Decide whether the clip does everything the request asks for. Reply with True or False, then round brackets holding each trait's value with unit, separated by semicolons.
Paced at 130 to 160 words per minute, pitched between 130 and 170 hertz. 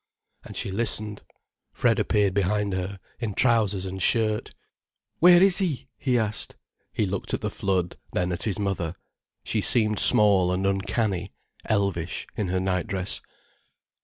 False (145 wpm; 100 Hz)